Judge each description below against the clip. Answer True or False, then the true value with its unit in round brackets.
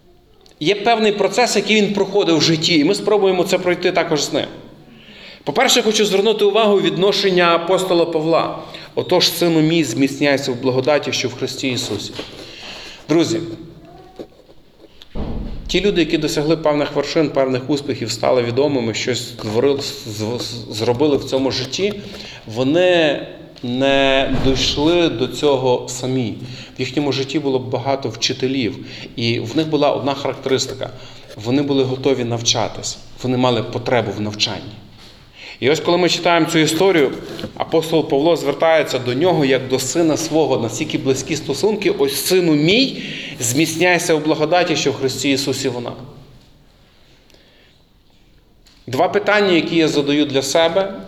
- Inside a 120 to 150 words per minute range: True (135 wpm)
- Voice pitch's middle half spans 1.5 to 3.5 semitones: False (4.6 semitones)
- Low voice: False (145 Hz)